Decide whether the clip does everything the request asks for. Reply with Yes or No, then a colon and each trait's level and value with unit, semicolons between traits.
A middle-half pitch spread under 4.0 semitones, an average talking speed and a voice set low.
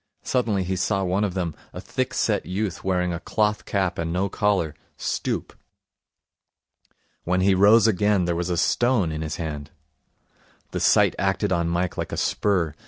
Yes: average, 2.9 semitones; average, 170 wpm; very low, 95 Hz